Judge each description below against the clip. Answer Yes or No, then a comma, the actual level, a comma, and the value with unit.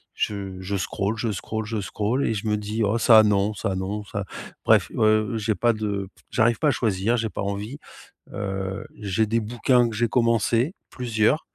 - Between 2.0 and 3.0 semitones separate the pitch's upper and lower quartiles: Yes, narrow, 2.4 semitones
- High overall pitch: No, low, 110 Hz